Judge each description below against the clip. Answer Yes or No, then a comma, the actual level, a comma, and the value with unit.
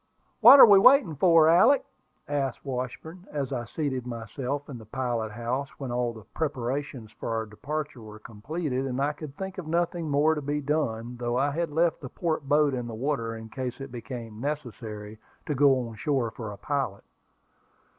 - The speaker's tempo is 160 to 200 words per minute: Yes, average, 190 wpm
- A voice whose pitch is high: No, low, 135 Hz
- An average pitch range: Yes, average, 4.3 semitones